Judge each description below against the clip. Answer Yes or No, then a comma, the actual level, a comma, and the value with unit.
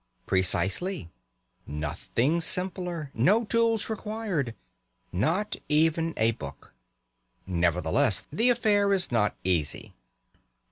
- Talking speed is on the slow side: Yes, slow, 90 wpm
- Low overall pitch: No, medium, 160 Hz